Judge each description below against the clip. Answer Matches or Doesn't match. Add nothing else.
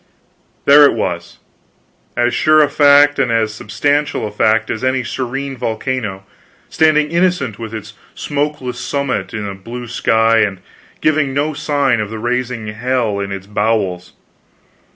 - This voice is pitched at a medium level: Doesn't match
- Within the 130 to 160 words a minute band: Matches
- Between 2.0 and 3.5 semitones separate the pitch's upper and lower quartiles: Doesn't match